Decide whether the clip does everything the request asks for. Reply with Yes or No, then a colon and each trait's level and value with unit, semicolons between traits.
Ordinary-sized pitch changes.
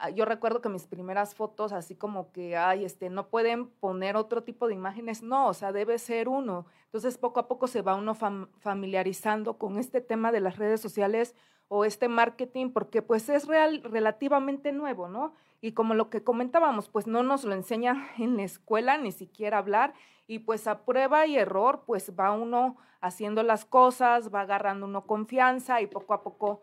Yes: average, 3.4 semitones